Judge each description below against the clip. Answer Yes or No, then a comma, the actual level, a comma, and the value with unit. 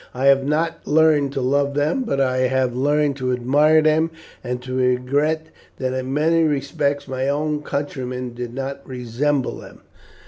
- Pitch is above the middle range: No, medium, 140 Hz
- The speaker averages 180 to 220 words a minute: No, average, 165 wpm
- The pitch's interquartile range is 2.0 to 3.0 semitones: Yes, narrow, 2.6 semitones